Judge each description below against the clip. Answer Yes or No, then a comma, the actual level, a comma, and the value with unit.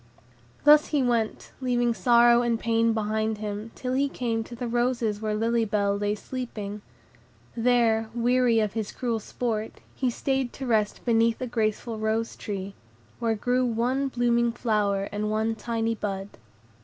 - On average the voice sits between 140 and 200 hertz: No, high, 230 Hz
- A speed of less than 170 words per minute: Yes, average, 155 wpm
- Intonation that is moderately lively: No, narrow, 2.1 semitones